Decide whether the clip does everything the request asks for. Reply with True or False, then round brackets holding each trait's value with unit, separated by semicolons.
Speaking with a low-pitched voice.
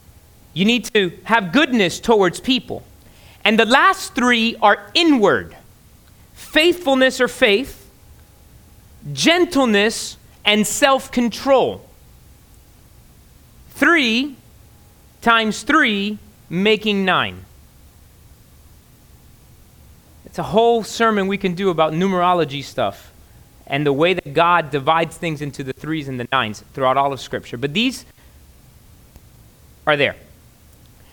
False (195 Hz)